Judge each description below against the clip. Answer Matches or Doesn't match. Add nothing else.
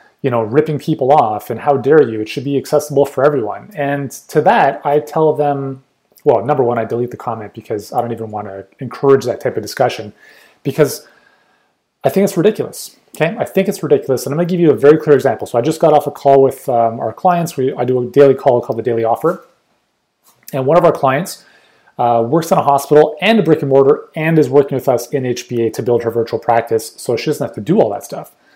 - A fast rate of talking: Matches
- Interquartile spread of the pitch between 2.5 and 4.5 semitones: Matches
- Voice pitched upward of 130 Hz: Matches